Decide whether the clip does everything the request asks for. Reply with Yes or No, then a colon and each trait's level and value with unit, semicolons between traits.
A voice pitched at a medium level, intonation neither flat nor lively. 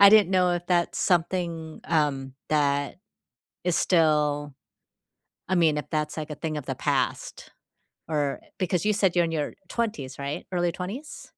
Yes: medium, 165 Hz; average, 3.4 semitones